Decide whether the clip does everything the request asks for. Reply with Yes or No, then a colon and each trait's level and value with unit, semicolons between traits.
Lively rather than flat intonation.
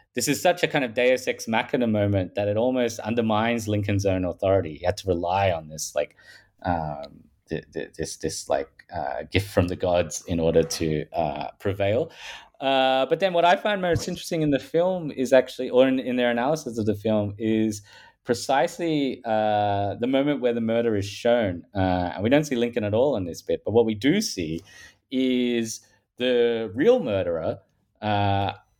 No: average, 4.9 semitones